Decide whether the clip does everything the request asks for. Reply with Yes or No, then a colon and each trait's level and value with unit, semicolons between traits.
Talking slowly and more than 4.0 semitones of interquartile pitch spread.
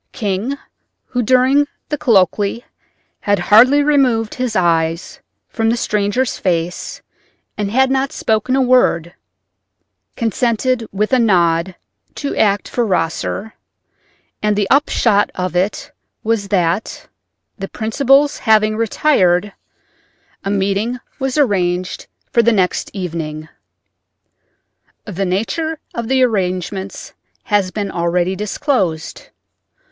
Yes: slow, 110 wpm; average, 5.2 semitones